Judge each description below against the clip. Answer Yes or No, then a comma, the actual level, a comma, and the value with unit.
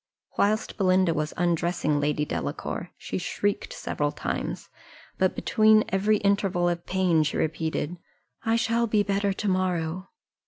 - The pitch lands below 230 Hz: Yes, medium, 185 Hz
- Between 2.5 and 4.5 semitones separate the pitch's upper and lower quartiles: Yes, average, 3.5 semitones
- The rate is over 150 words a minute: No, slow, 135 wpm